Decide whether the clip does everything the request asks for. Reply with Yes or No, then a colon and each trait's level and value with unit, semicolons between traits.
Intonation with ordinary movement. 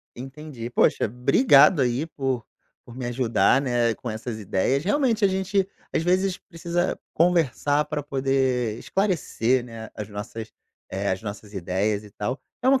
No: wide, 6.8 semitones